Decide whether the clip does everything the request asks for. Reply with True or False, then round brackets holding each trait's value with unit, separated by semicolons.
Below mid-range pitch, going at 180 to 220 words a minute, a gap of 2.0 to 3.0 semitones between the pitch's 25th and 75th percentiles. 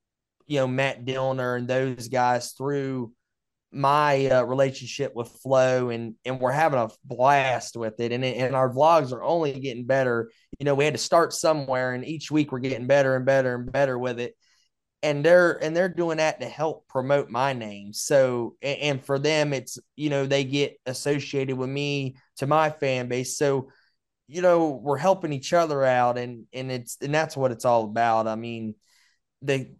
True (130 Hz; 195 wpm; 2.4 semitones)